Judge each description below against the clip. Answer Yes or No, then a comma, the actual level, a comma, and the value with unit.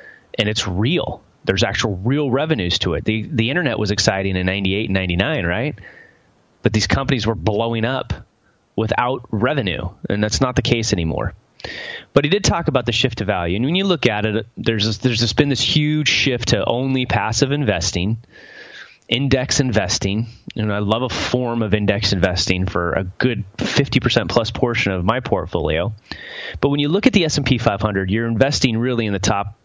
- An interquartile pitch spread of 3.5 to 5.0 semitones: Yes, average, 4.0 semitones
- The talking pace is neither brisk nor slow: Yes, average, 190 wpm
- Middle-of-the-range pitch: No, low, 115 Hz